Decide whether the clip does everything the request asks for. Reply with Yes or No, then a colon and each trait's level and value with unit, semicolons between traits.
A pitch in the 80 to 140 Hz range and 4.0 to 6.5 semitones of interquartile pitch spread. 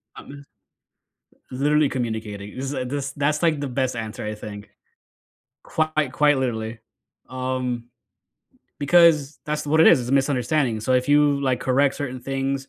No: low, 135 Hz; average, 2.8 semitones